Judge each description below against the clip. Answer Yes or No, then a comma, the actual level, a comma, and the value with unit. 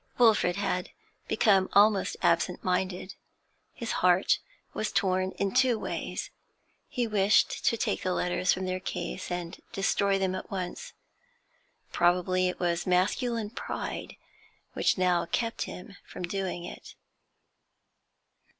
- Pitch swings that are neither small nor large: No, narrow, 2.2 semitones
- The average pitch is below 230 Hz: Yes, medium, 185 Hz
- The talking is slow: Yes, slow, 125 wpm